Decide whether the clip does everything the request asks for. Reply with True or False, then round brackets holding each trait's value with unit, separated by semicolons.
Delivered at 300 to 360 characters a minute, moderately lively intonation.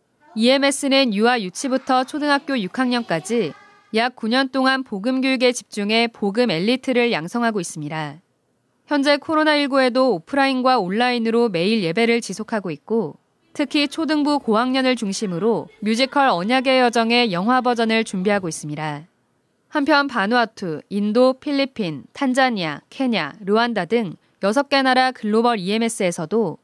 True (315 characters per minute; 4.1 semitones)